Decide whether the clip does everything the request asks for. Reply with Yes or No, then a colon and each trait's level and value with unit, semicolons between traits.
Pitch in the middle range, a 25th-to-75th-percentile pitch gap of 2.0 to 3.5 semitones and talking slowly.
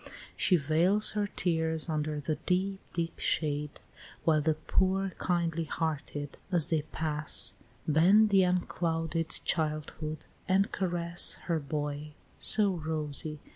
Yes: medium, 160 Hz; average, 2.8 semitones; slow, 120 wpm